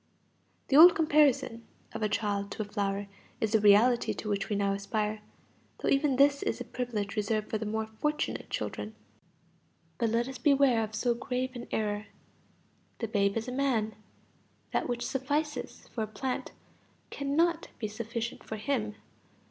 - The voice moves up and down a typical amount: Yes, average, 3.9 semitones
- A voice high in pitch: Yes, high, 225 Hz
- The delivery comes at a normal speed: Yes, average, 165 wpm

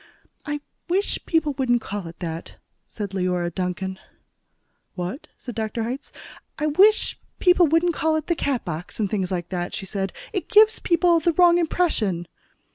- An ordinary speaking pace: Yes, average, 160 wpm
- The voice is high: Yes, high, 245 Hz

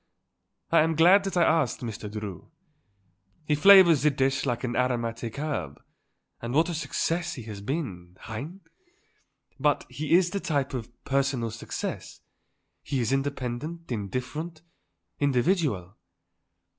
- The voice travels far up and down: Yes, wide, 5.7 semitones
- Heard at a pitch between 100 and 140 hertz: Yes, low, 135 Hz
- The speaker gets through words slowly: Yes, slow, 130 wpm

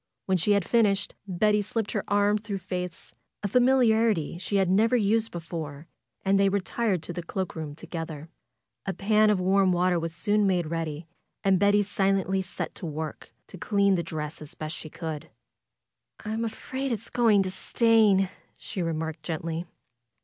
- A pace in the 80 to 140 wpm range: No, average, 170 wpm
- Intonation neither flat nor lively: Yes, average, 4.0 semitones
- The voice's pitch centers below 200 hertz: Yes, high, 190 Hz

